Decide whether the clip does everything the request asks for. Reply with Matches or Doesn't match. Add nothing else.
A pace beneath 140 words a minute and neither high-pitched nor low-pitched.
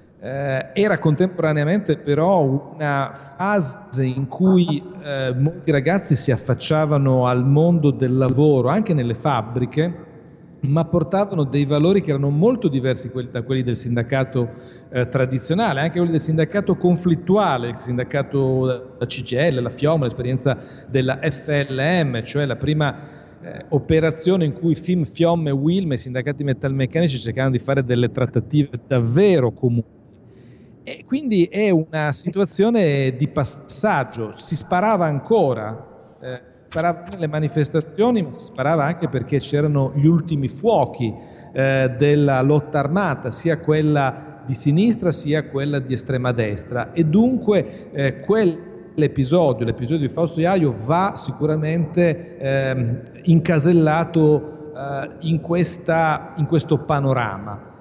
Matches